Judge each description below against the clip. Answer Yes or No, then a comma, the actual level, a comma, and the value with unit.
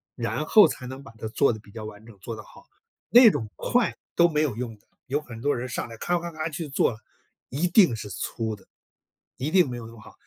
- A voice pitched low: Yes, low, 125 Hz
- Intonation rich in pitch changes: Yes, wide, 5.8 semitones